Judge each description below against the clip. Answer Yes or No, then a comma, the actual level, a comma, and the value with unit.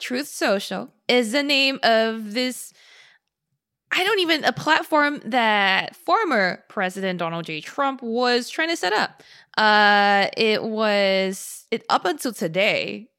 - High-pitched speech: Yes, high, 230 Hz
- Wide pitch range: Yes, wide, 5.9 semitones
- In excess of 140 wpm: No, slow, 135 wpm